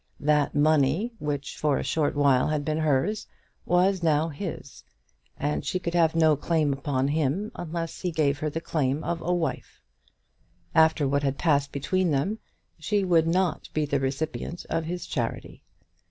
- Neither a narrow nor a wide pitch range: Yes, average, 3.0 semitones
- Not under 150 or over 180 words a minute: Yes, average, 170 wpm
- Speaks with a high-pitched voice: No, medium, 155 Hz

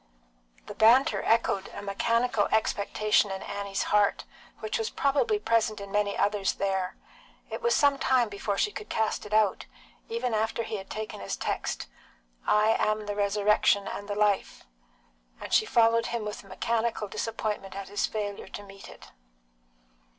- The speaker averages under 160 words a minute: No, average, 165 wpm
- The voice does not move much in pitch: Yes, narrow, 2.1 semitones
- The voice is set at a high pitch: Yes, high, 210 Hz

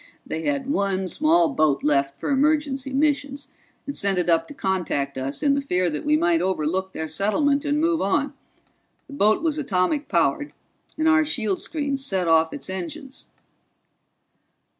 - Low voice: No, very high, 265 Hz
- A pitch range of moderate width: No, wide, 8.3 semitones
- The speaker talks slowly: No, average, 165 wpm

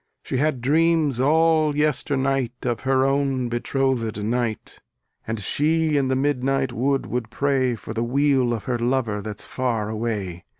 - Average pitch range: Yes, average, 3.1 semitones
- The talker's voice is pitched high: No, low, 130 Hz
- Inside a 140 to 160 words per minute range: Yes, average, 155 wpm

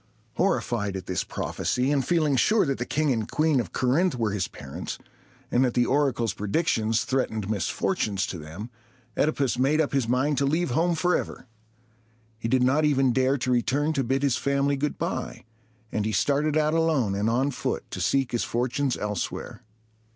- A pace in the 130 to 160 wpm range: No, average, 180 wpm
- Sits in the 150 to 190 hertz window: No, low, 130 Hz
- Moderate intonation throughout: Yes, average, 4.3 semitones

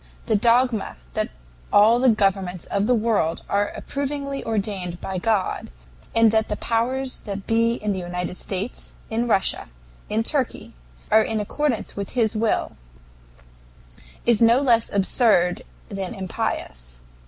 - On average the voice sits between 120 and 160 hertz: No, high, 220 Hz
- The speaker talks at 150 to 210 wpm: No, average, 140 wpm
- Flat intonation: No, average, 3.3 semitones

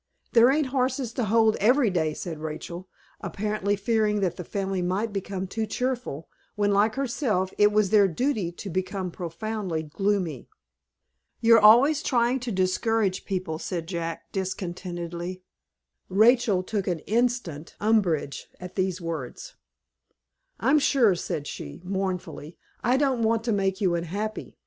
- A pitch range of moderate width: Yes, average, 4.1 semitones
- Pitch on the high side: Yes, high, 200 Hz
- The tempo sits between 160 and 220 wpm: No, average, 140 wpm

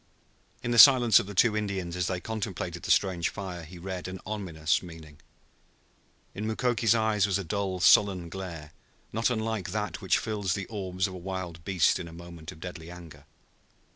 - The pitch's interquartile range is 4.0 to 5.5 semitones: No, average, 3.4 semitones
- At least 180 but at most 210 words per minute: Yes, average, 185 wpm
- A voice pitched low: Yes, very low, 95 Hz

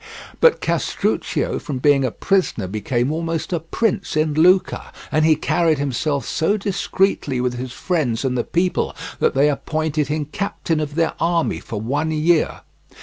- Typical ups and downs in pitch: Yes, average, 3.7 semitones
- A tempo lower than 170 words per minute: Yes, average, 160 wpm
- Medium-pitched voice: Yes, medium, 155 Hz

